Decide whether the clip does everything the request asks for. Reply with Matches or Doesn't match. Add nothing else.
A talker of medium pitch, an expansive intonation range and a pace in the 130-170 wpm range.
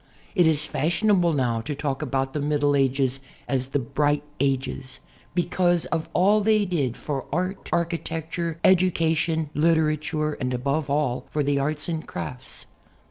Doesn't match